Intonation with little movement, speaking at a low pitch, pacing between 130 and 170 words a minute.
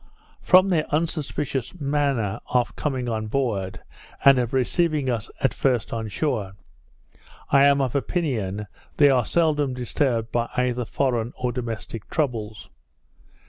No: average, 3.9 semitones; low, 125 Hz; slow, 135 wpm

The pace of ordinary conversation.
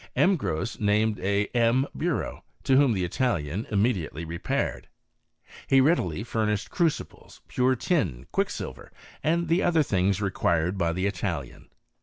Yes: average, 145 wpm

